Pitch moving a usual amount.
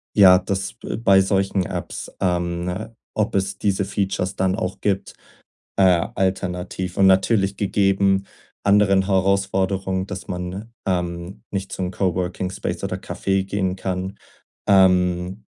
No: narrow, 1.1 semitones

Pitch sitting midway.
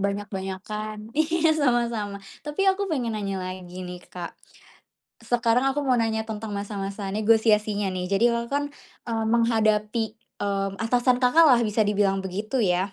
No: high, 215 Hz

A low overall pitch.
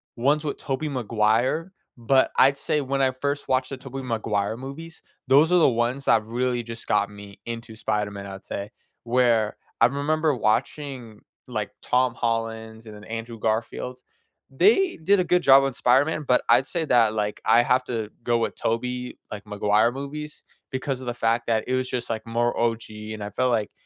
Yes: low, 120 Hz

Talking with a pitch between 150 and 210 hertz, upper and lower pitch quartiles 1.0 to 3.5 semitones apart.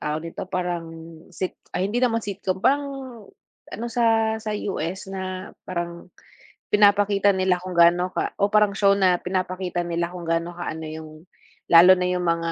Yes: medium, 185 Hz; average, 2.7 semitones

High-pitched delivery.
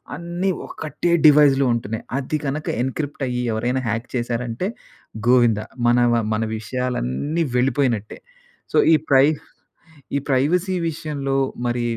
No: low, 130 Hz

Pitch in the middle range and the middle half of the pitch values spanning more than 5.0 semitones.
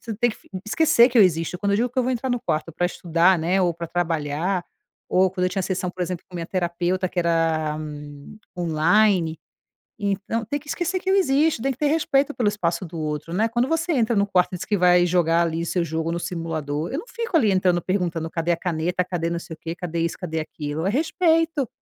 Yes: medium, 180 Hz; wide, 5.4 semitones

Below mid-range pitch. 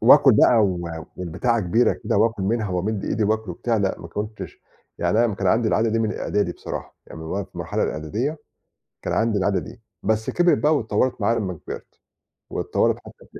Yes: low, 110 Hz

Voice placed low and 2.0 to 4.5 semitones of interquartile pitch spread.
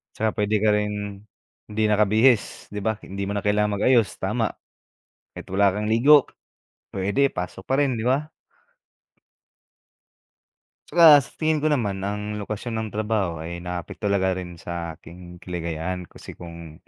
Yes: low, 105 Hz; average, 3.4 semitones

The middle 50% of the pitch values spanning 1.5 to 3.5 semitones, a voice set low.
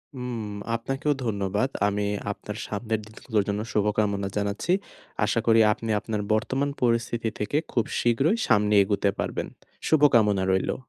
Yes: average, 2.7 semitones; low, 110 Hz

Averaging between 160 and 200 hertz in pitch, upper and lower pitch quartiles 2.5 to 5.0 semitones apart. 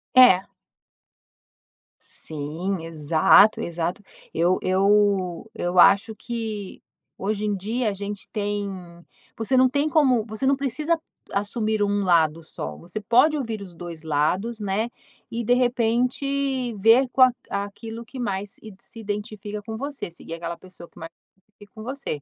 No: high, 210 Hz; average, 4.3 semitones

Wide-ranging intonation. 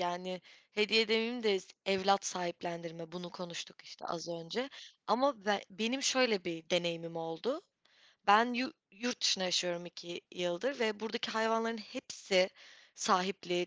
No: average, 4.5 semitones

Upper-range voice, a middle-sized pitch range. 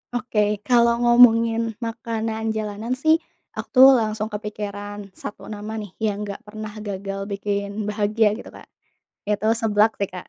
No: high, 215 Hz; narrow, 1.8 semitones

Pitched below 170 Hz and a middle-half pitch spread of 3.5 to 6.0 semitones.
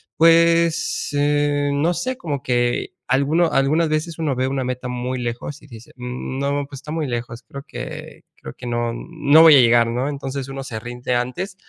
Yes: medium, 140 Hz; average, 3.8 semitones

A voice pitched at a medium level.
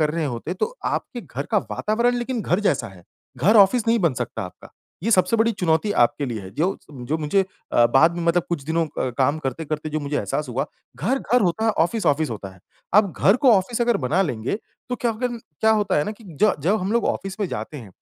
Yes: medium, 175 Hz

